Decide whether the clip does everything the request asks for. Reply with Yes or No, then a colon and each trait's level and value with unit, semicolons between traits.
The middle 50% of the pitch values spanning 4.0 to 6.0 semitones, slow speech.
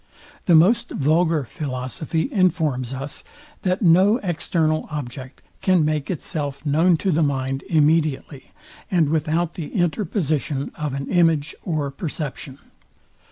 No: average, 3.4 semitones; slow, 120 wpm